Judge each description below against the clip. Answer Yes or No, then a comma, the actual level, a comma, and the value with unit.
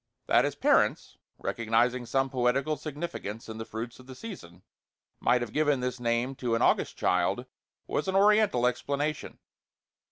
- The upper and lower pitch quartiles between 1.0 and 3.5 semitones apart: No, average, 3.9 semitones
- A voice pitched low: Yes, low, 125 Hz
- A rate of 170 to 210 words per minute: No, average, 155 wpm